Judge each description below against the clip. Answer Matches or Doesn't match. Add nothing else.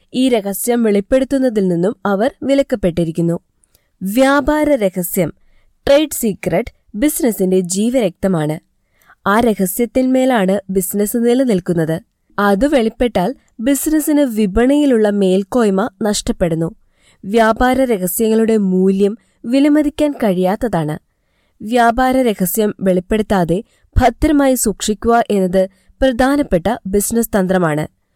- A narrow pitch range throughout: Doesn't match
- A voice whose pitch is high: Matches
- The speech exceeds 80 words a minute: Doesn't match